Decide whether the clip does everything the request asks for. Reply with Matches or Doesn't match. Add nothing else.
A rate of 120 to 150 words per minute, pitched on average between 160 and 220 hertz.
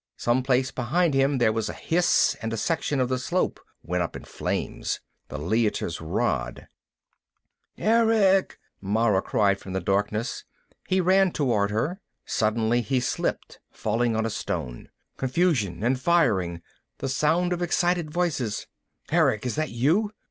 Doesn't match